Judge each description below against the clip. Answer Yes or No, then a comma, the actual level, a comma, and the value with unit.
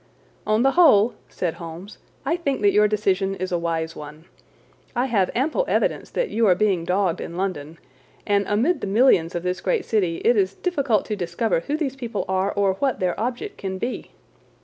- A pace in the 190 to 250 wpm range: Yes, average, 195 wpm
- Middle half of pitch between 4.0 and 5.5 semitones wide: Yes, average, 5.1 semitones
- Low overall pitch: No, high, 200 Hz